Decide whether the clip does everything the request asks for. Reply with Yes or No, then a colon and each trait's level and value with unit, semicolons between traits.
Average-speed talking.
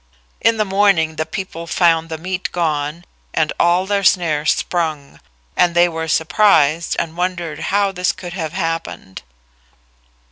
Yes: average, 145 wpm